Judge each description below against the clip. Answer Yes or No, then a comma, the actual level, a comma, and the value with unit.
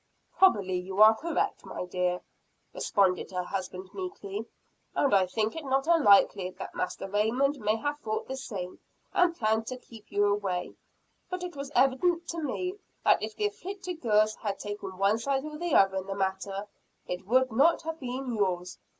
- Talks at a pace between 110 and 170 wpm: No, average, 180 wpm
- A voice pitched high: Yes, high, 220 Hz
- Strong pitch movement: Yes, wide, 6.9 semitones